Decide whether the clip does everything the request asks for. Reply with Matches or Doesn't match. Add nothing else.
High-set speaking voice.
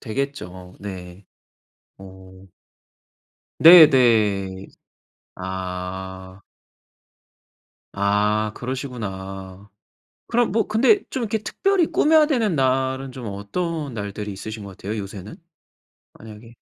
Doesn't match